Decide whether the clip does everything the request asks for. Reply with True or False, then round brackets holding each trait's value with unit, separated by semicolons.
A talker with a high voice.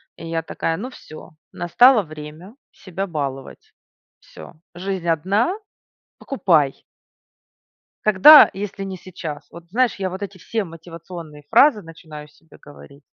False (175 Hz)